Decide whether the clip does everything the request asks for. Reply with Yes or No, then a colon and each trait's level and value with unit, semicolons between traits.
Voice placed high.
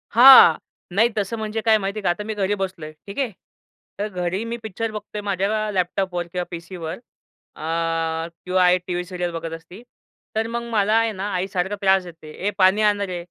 Yes: high, 195 Hz